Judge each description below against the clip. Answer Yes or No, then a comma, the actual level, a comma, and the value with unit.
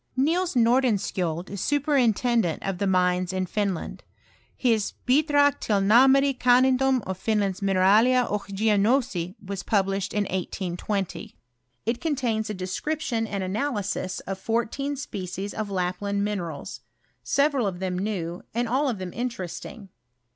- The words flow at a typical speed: No, slow, 125 wpm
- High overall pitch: Yes, high, 210 Hz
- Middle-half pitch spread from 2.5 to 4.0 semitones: No, average, 5.0 semitones